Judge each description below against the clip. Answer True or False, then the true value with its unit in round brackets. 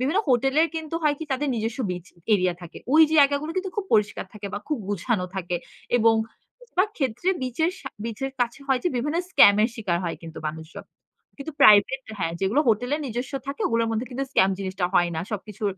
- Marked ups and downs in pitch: True (5.9 semitones)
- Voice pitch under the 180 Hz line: False (235 Hz)